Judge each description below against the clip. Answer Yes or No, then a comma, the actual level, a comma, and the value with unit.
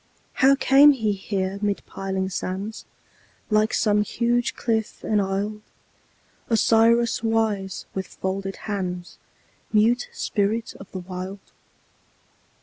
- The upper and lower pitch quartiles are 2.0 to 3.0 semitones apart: Yes, average, 2.7 semitones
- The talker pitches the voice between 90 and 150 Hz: No, high, 210 Hz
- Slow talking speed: Yes, slow, 105 wpm